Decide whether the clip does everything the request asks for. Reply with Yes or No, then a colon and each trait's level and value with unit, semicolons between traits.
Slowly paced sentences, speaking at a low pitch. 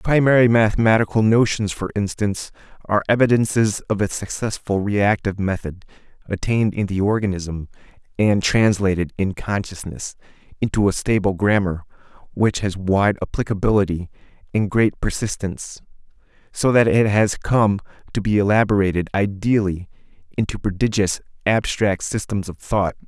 Yes: slow, 120 wpm; low, 100 Hz